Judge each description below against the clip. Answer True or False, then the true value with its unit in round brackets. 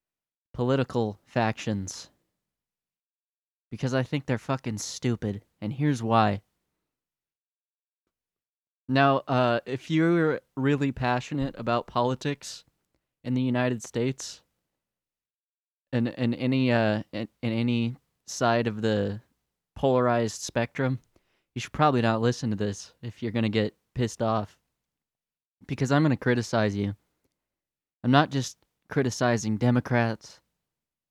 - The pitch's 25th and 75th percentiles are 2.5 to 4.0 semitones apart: True (2.9 semitones)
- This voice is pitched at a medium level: False (120 Hz)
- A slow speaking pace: True (110 wpm)